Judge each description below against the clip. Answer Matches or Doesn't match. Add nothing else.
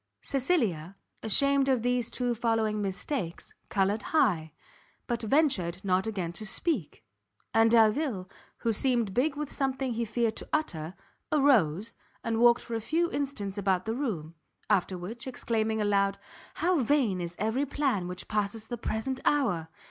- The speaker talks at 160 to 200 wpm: Doesn't match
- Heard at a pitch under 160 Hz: Doesn't match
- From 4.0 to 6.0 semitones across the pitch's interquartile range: Matches